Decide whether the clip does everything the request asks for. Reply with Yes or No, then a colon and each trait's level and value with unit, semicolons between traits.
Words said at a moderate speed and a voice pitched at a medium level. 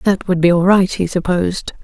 No: fast, 230 wpm; medium, 180 Hz